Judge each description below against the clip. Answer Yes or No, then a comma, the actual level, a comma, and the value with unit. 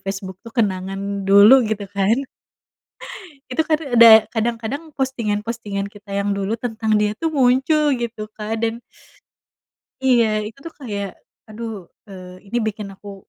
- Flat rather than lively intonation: No, average, 3.2 semitones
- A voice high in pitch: Yes, high, 220 Hz